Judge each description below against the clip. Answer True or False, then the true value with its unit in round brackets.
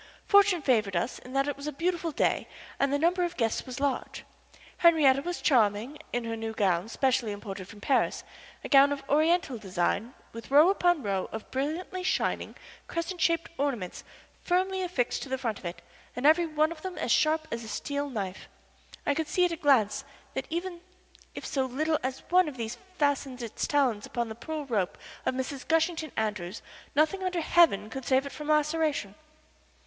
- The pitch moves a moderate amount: False (5.9 semitones)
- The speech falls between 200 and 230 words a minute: False (190 wpm)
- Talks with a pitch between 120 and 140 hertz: False (280 Hz)